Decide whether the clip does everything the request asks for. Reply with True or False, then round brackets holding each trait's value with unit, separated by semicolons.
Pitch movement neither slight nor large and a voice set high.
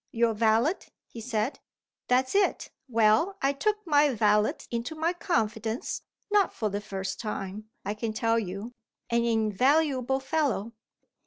True (4.7 semitones; 230 Hz)